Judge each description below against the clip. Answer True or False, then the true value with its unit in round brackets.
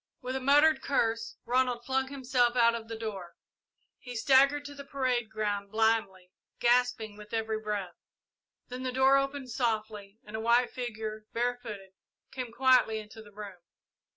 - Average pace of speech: True (155 wpm)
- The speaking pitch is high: True (235 Hz)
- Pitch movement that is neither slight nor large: True (3.0 semitones)